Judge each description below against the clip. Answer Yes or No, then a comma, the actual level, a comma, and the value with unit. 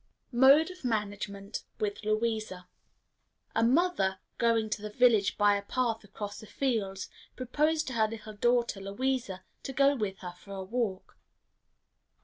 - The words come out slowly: No, average, 145 wpm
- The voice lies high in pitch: Yes, high, 220 Hz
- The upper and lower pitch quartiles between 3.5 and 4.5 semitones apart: Yes, average, 3.8 semitones